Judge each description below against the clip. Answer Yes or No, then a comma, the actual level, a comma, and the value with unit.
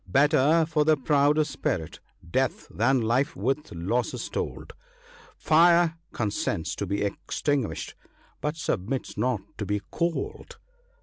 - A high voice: No, low, 135 Hz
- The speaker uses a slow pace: Yes, slow, 125 wpm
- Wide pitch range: Yes, wide, 5.8 semitones